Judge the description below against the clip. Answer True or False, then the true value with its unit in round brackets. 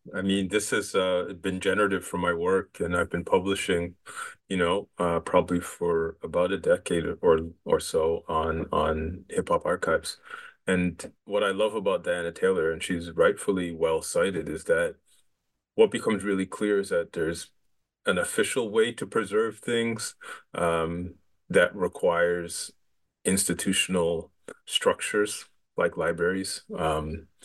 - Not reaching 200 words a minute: True (140 wpm)